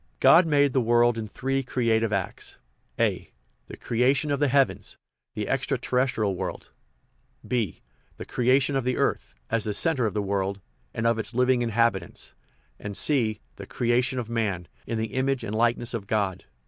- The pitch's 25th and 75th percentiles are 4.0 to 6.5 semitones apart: No, average, 3.2 semitones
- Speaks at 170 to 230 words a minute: Yes, average, 175 wpm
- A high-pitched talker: No, low, 120 Hz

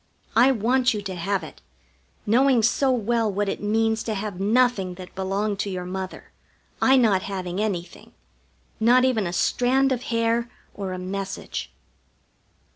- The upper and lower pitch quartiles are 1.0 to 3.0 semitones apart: No, average, 4.0 semitones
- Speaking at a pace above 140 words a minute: Yes, average, 155 wpm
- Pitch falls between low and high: No, high, 210 Hz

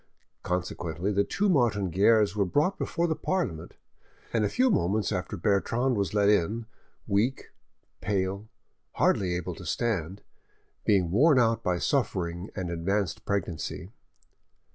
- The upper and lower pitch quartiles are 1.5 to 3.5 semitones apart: No, average, 4.3 semitones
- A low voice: Yes, low, 100 Hz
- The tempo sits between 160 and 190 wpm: No, slow, 135 wpm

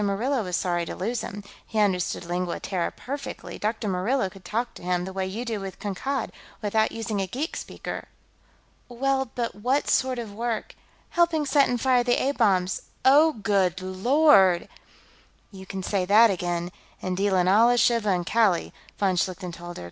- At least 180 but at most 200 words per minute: Yes, average, 185 wpm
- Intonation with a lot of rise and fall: No, average, 4.7 semitones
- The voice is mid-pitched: No, high, 205 Hz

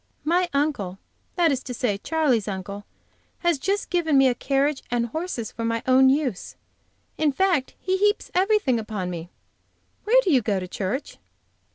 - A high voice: Yes, very high, 265 Hz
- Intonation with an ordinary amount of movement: No, wide, 7.3 semitones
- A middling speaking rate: Yes, average, 170 wpm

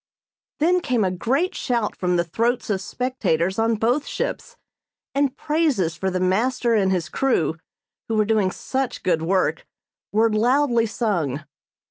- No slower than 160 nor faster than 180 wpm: No, average, 150 wpm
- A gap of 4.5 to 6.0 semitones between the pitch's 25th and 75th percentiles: Yes, wide, 5.5 semitones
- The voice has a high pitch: Yes, high, 220 Hz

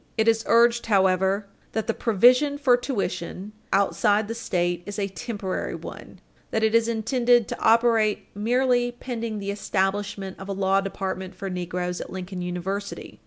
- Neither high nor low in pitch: No, high, 205 Hz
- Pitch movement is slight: No, average, 3.4 semitones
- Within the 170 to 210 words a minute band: No, average, 160 wpm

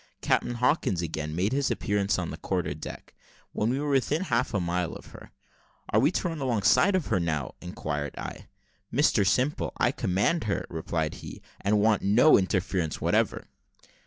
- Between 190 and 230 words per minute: No, average, 180 wpm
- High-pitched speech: No, low, 100 Hz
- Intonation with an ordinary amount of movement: No, wide, 7.0 semitones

